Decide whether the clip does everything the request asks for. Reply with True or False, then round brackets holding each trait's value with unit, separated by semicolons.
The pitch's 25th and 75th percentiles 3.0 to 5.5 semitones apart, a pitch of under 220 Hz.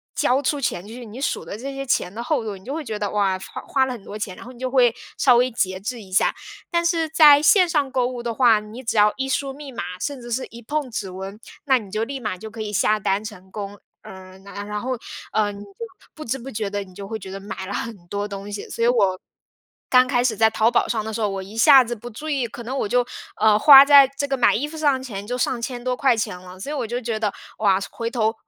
False (4.3 semitones; 230 Hz)